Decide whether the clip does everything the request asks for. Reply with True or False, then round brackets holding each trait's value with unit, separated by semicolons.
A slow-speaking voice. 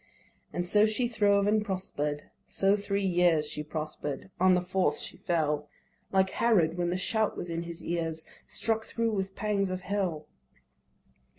False (165 wpm)